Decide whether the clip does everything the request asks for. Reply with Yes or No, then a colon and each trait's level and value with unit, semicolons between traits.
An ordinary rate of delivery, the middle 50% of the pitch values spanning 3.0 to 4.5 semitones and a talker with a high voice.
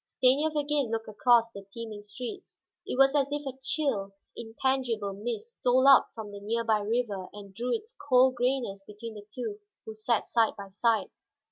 Yes: average, 180 wpm; average, 4.1 semitones; high, 230 Hz